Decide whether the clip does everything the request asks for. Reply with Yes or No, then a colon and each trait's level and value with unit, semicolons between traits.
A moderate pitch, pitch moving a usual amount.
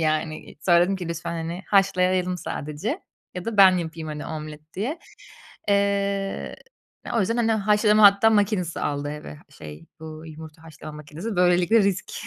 Yes: medium, 180 Hz; average, 4.4 semitones